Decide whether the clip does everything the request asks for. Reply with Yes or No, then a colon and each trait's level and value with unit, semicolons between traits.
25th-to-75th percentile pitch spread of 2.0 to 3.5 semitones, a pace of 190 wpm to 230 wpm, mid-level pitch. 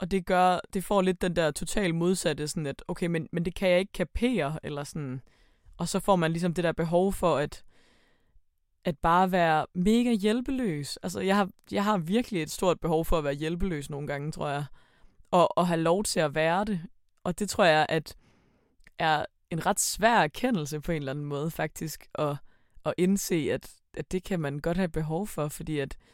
No: average, 3.9 semitones; average, 210 wpm; medium, 170 Hz